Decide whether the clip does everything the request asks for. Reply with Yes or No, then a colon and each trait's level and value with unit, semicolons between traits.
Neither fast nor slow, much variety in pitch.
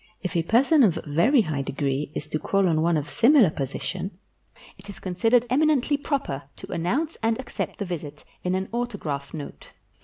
Yes: average, 185 wpm; wide, 7.8 semitones